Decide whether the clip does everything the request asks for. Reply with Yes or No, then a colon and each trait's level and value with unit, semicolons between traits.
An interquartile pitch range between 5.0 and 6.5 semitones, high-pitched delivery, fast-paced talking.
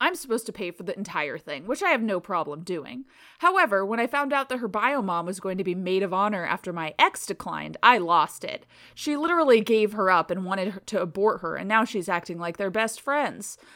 Yes: wide, 5.5 semitones; high, 205 Hz; fast, 240 wpm